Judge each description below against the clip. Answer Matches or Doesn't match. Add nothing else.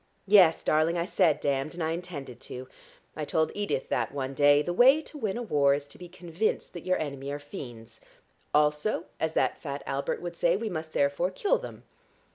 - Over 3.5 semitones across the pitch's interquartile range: Matches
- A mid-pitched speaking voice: Matches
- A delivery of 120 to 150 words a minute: Doesn't match